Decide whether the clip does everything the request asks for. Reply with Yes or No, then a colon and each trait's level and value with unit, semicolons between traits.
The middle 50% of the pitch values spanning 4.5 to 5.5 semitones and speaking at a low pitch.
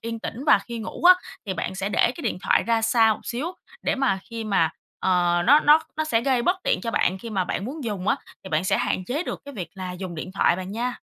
No: average, 5.0 semitones; high, 225 Hz